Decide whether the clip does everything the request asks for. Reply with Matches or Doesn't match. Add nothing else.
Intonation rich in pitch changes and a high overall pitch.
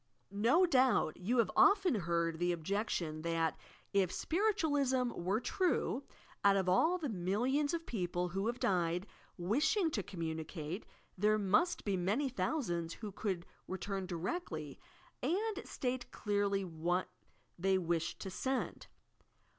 Matches